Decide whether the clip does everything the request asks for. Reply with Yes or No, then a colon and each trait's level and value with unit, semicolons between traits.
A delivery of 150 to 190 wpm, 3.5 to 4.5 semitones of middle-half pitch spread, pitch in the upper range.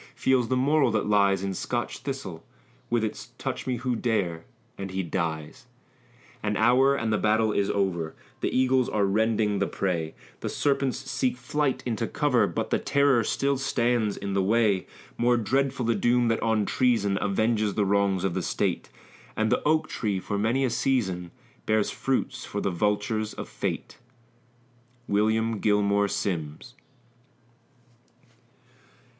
No: average, 155 wpm; average, 3.9 semitones; low, 110 Hz